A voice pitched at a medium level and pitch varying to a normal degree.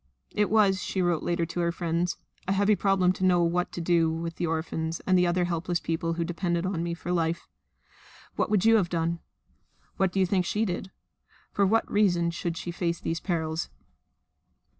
No: medium, 175 Hz; narrow, 2.0 semitones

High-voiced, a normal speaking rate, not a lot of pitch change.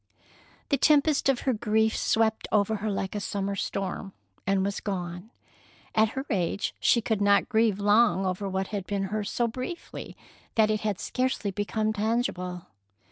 Yes: high, 210 Hz; average, 165 wpm; narrow, 2.3 semitones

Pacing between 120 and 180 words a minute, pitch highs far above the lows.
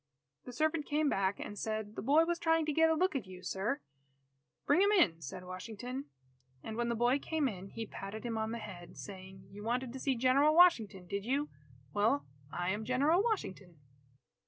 No: average, 200 wpm; wide, 6.9 semitones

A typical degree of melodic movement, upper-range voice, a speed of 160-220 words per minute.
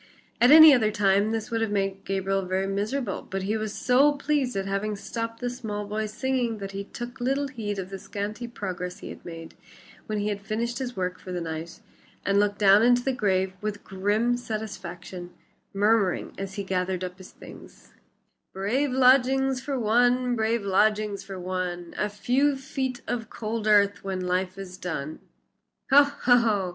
Yes: average, 4.0 semitones; high, 210 Hz; average, 175 wpm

